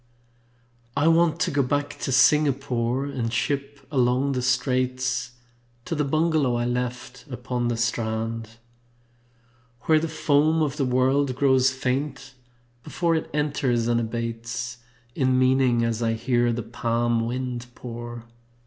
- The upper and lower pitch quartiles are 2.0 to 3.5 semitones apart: Yes, average, 2.9 semitones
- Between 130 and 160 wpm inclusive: Yes, slow, 135 wpm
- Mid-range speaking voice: No, low, 125 Hz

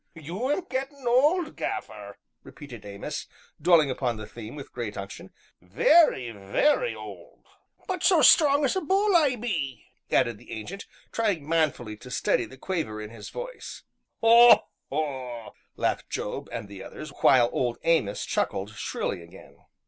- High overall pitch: No, medium, 150 Hz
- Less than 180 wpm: Yes, average, 155 wpm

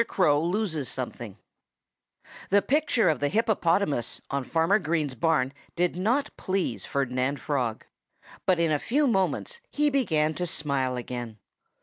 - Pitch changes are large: Yes, wide, 6.4 semitones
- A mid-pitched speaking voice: Yes, medium, 160 Hz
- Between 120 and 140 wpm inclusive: Yes, slow, 135 wpm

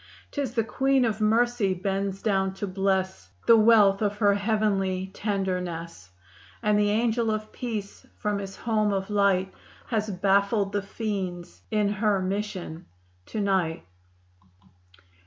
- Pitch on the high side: Yes, high, 200 Hz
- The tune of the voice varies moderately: No, narrow, 2.0 semitones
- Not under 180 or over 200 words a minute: No, slow, 135 wpm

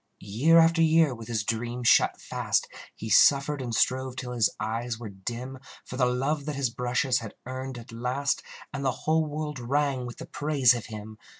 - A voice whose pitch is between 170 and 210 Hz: No, low, 125 Hz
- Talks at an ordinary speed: Yes, average, 195 wpm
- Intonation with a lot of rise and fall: No, average, 3.2 semitones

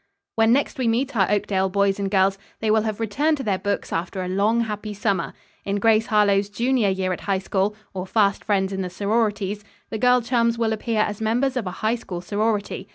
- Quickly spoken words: Yes, fast, 220 wpm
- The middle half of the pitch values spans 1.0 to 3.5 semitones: Yes, narrow, 2.5 semitones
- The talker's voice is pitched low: No, high, 210 Hz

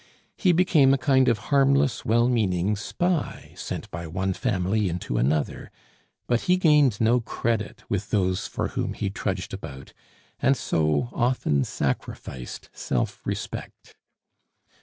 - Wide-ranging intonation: Yes, wide, 6.6 semitones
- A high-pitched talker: No, low, 110 Hz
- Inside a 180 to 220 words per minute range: No, slow, 135 wpm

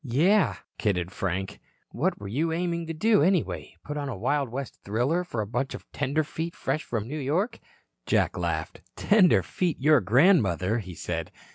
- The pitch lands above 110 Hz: Yes, medium, 140 Hz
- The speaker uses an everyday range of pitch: No, wide, 7.5 semitones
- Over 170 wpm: No, average, 165 wpm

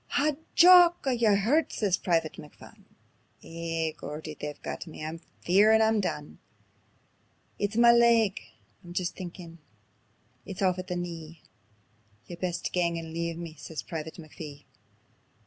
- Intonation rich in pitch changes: No, average, 4.6 semitones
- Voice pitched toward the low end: No, medium, 175 Hz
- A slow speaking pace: No, average, 145 wpm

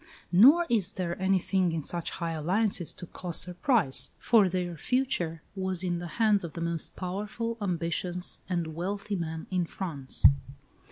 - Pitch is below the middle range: No, medium, 180 Hz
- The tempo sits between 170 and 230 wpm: No, average, 155 wpm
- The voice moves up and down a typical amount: Yes, average, 3.0 semitones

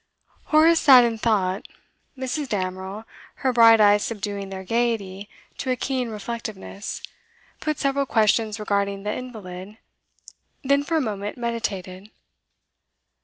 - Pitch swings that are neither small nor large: Yes, average, 4.0 semitones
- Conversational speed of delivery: No, slow, 120 wpm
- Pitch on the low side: No, high, 220 Hz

